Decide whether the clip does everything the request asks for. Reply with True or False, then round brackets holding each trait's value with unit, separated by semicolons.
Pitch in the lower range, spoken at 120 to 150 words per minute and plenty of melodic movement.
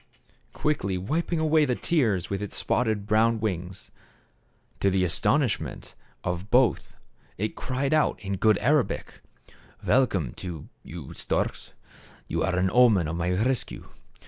True (105 Hz; 140 wpm; 5.7 semitones)